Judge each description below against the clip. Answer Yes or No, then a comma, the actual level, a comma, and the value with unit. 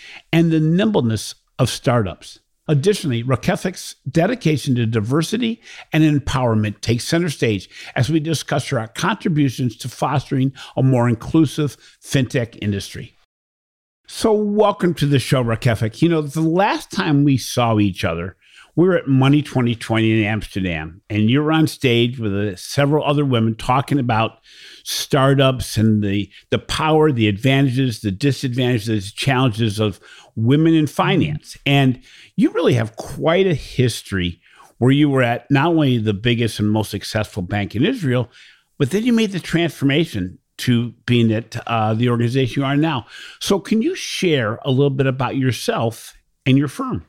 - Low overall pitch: Yes, low, 130 Hz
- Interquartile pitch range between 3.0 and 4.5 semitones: No, average, 5.2 semitones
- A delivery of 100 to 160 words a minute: Yes, average, 155 wpm